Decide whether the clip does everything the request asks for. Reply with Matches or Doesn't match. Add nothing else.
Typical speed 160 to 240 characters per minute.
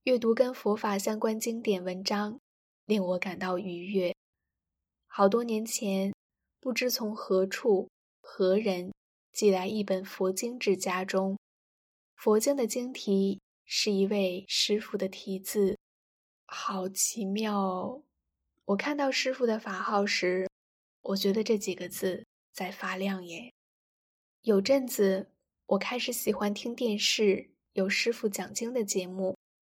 Matches